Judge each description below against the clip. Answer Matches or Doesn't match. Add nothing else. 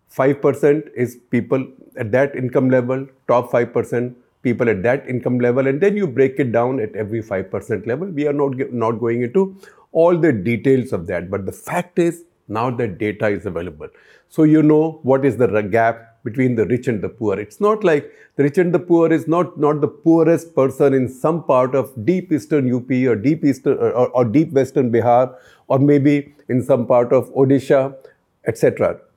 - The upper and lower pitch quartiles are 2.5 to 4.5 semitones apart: Matches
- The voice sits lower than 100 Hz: Doesn't match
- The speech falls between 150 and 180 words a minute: Doesn't match